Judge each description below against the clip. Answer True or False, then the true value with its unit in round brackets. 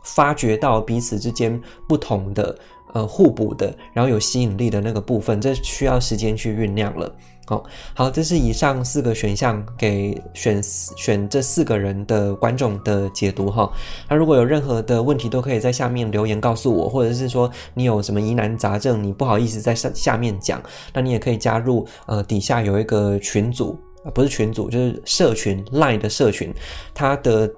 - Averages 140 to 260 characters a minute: False (290 characters per minute)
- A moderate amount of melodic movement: True (3.3 semitones)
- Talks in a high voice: False (115 Hz)